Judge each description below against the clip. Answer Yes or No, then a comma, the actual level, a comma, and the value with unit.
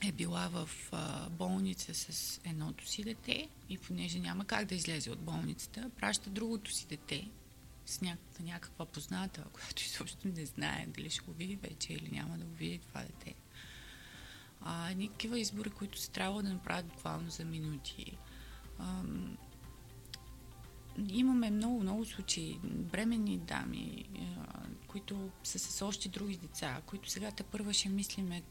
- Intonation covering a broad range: No, average, 4.1 semitones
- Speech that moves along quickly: No, average, 145 wpm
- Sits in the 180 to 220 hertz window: Yes, high, 190 Hz